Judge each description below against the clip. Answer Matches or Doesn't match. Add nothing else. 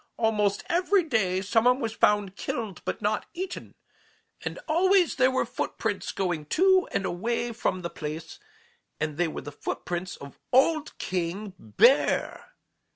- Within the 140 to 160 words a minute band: Matches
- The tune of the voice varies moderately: Doesn't match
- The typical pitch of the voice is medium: Doesn't match